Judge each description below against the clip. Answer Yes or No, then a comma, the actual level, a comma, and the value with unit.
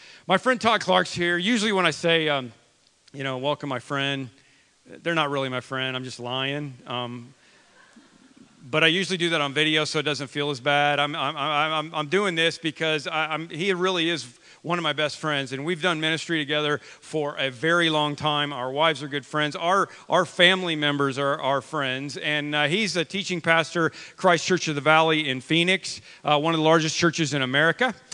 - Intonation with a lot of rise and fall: No, average, 3.2 semitones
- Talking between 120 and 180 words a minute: No, fast, 205 wpm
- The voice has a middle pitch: Yes, medium, 155 Hz